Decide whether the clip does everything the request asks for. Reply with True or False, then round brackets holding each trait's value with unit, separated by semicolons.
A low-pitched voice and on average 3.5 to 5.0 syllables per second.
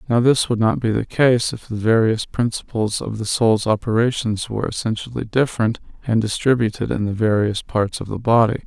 False (115 Hz; 5.4 syllables/s)